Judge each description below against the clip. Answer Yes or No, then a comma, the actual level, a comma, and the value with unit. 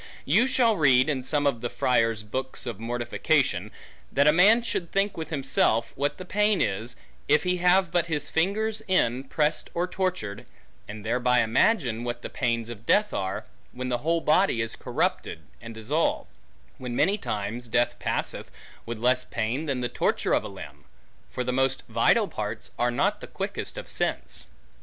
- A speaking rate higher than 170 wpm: Yes, average, 180 wpm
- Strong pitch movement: Yes, wide, 6.5 semitones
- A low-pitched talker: Yes, low, 130 Hz